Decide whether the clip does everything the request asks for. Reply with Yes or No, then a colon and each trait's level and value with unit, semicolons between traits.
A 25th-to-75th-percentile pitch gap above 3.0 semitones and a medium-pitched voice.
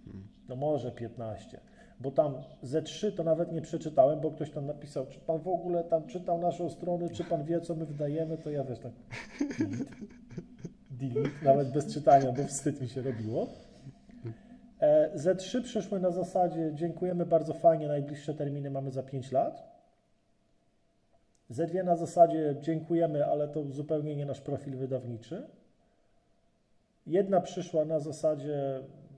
Yes: average, 3.8 semitones; medium, 155 Hz